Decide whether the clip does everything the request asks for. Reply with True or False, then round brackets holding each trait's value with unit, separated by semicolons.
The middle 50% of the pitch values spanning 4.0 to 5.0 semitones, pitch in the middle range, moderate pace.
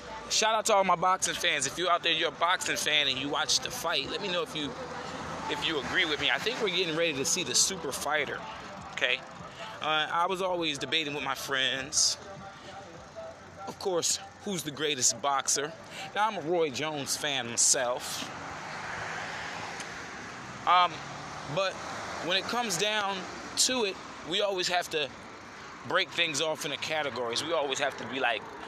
True (4.3 semitones; 160 Hz; 180 wpm)